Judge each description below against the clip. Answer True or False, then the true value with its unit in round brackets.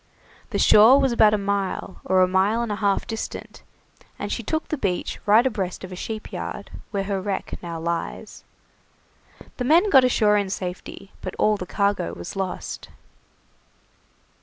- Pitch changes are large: False (3.0 semitones)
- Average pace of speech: True (170 wpm)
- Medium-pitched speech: False (200 Hz)